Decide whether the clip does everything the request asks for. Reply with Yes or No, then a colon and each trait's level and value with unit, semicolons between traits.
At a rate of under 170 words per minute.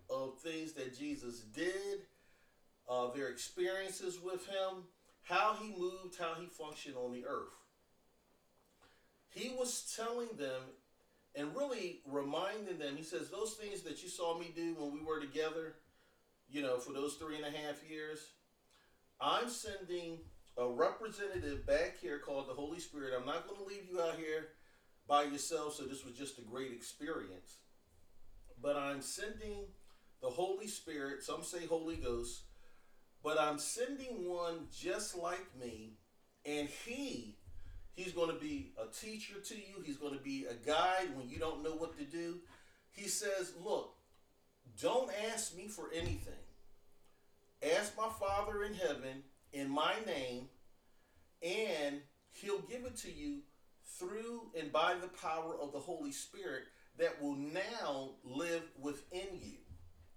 Yes: average, 155 wpm